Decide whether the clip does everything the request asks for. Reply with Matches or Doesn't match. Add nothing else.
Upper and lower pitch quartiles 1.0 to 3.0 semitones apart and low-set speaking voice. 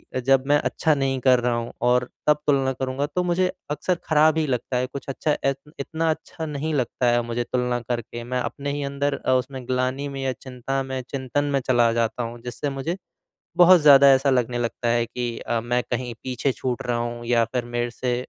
Matches